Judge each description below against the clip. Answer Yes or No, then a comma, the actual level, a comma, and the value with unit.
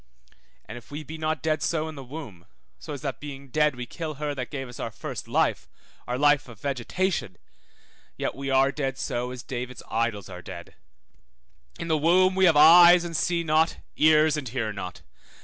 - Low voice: No, medium, 145 Hz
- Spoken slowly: No, average, 200 wpm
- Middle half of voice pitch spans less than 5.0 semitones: Yes, average, 4.1 semitones